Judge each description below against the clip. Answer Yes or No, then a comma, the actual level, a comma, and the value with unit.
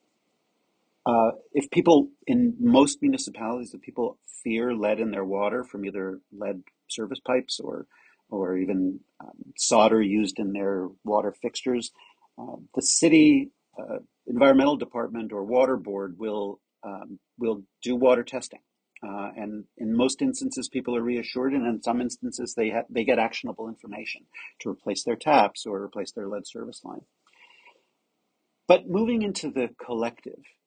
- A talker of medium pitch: No, low, 120 Hz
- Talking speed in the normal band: Yes, average, 150 wpm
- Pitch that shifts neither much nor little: No, wide, 6.8 semitones